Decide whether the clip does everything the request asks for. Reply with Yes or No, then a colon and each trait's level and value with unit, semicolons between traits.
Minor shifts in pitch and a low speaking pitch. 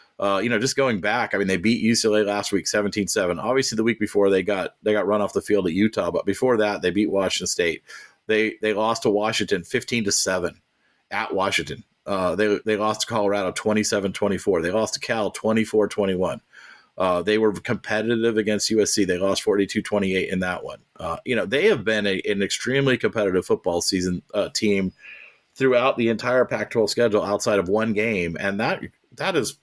Yes: narrow, 2.0 semitones; low, 105 Hz